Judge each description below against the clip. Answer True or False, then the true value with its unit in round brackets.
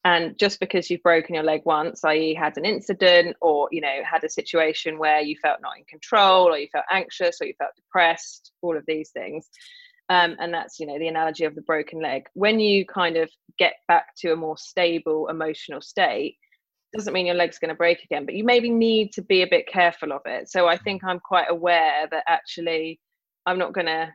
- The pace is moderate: False (225 wpm)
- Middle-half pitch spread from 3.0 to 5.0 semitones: True (3.8 semitones)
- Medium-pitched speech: True (170 Hz)